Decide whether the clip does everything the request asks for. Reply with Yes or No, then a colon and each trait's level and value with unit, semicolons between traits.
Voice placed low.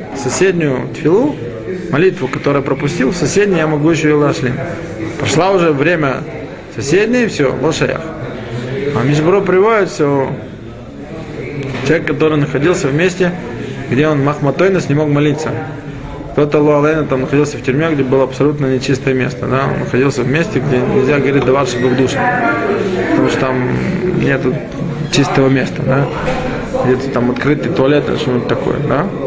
No: medium, 145 Hz